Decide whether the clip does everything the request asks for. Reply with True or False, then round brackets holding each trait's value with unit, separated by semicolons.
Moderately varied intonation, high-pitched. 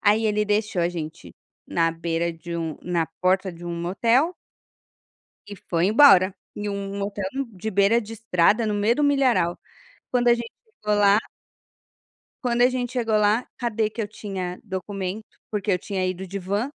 True (3.8 semitones; 205 Hz)